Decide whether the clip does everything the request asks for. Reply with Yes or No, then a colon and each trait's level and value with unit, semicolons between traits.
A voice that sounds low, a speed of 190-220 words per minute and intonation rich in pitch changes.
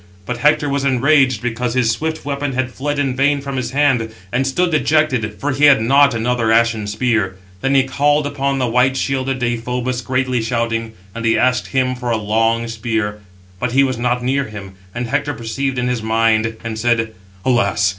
No: low, 125 Hz; average, 195 wpm; average, 3.2 semitones